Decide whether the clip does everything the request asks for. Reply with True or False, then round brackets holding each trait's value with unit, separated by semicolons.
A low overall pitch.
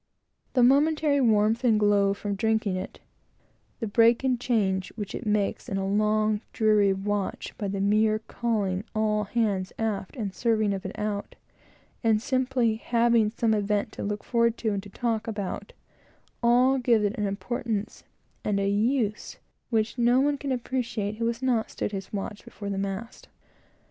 False (215 Hz)